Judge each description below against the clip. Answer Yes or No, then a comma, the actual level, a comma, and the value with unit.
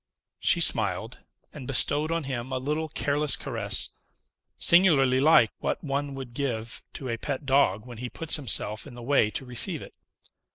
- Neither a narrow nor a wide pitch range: Yes, average, 3.3 semitones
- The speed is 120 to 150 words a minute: No, average, 170 wpm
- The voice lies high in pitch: No, low, 135 Hz